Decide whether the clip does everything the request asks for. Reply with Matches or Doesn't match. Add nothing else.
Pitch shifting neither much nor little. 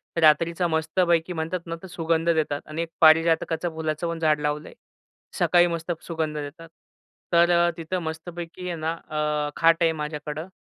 Doesn't match